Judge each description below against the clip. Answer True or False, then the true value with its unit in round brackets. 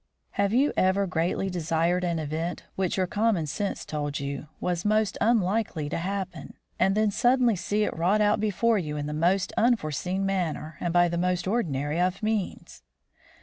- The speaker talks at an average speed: True (175 wpm)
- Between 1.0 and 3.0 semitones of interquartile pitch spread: False (4.0 semitones)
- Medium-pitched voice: True (180 Hz)